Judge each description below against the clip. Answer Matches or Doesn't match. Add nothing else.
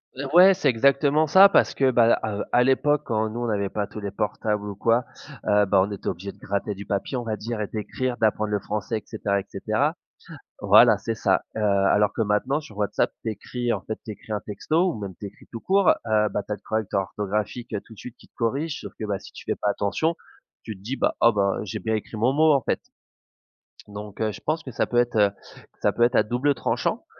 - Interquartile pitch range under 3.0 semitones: Doesn't match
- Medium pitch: Doesn't match